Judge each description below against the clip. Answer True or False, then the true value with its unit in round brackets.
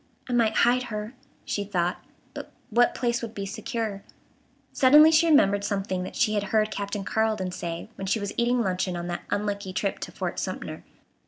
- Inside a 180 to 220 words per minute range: True (185 wpm)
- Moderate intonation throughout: True (3.3 semitones)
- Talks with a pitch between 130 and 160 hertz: False (210 Hz)